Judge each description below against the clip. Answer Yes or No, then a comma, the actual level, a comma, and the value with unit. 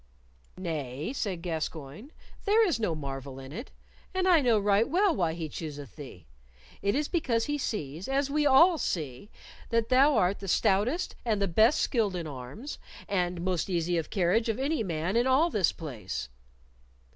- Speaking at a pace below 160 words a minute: No, average, 175 wpm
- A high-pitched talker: Yes, high, 200 Hz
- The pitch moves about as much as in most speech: No, wide, 8.7 semitones